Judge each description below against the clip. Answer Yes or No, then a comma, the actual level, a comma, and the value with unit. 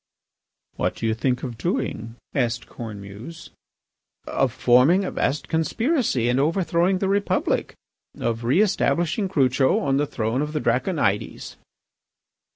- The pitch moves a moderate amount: No, wide, 6.6 semitones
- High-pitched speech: No, low, 135 Hz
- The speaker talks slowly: Yes, slow, 130 wpm